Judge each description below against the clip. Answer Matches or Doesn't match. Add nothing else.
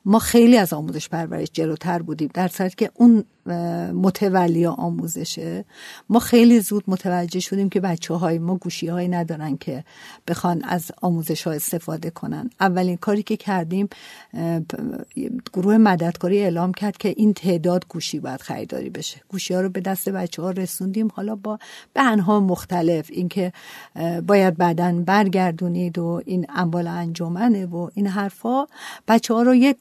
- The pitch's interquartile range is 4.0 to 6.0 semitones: Doesn't match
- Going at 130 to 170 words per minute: Matches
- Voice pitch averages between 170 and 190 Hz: Matches